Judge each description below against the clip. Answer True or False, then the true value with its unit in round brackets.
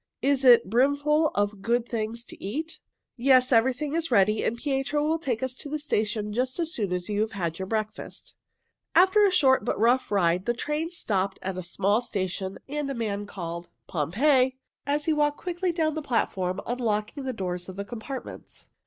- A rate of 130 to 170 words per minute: False (195 wpm)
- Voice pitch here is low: False (240 Hz)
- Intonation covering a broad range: True (6.2 semitones)